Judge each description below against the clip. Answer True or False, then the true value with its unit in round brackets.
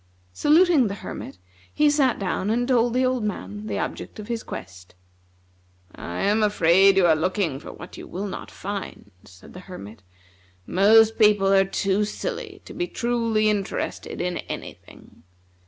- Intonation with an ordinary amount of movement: True (4.6 semitones)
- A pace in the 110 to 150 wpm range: False (165 wpm)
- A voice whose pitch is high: True (205 Hz)